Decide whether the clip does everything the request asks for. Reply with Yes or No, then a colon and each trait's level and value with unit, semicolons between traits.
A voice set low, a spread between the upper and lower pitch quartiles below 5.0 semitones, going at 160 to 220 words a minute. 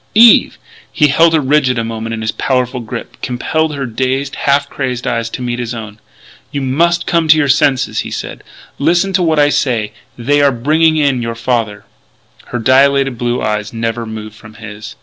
Yes: low, 130 Hz; average, 4.0 semitones; average, 190 wpm